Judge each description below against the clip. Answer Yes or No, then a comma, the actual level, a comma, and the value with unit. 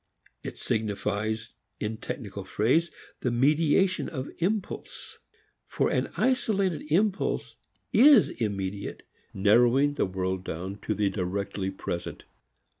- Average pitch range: No, wide, 8.1 semitones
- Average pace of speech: No, slow, 110 wpm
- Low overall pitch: Yes, low, 110 Hz